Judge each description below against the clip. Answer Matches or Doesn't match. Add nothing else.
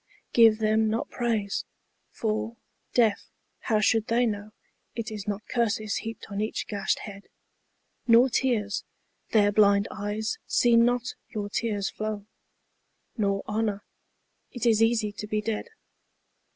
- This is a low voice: Doesn't match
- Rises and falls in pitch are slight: Matches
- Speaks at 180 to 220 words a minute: Doesn't match